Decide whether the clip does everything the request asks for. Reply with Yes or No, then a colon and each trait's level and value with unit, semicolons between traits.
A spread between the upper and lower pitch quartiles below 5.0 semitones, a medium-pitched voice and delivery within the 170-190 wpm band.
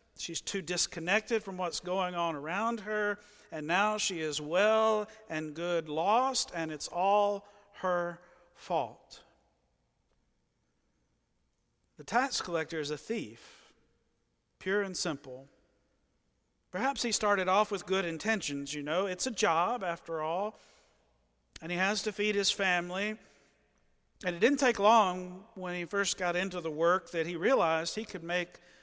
No: average, 4.1 semitones; medium, 180 Hz; average, 145 wpm